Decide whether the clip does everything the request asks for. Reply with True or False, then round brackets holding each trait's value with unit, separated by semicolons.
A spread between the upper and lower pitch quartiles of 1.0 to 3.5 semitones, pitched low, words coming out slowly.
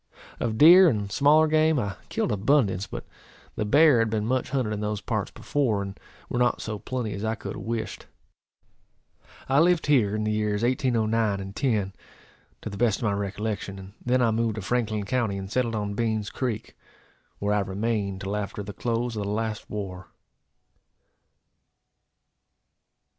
False (3.2 semitones; 110 Hz; 175 wpm)